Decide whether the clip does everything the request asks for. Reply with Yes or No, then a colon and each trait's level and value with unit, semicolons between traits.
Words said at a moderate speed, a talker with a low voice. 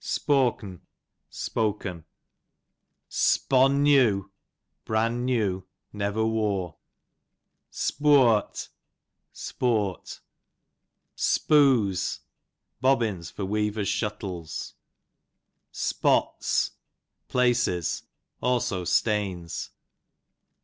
No: slow, 60 wpm; low, 105 Hz